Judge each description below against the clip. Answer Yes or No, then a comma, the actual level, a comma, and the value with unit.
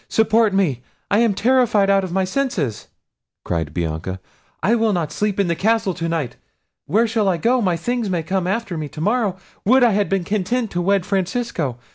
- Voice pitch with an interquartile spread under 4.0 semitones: No, average, 4.8 semitones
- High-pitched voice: Yes, high, 195 Hz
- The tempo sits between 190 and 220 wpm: Yes, average, 195 wpm